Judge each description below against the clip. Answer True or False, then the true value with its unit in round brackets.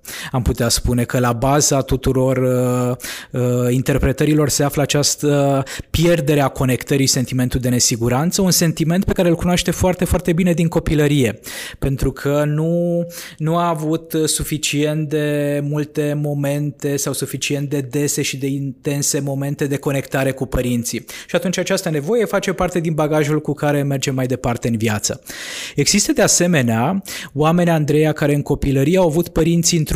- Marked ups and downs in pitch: False (3.4 semitones)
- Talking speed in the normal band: True (160 wpm)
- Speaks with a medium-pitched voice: True (145 Hz)